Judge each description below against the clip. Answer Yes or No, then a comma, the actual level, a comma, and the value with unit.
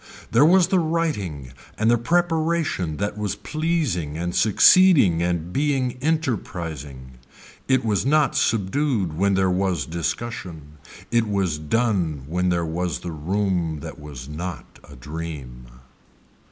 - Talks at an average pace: No, slow, 130 wpm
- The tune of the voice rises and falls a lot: Yes, wide, 8.4 semitones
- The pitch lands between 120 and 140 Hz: No, very low, 95 Hz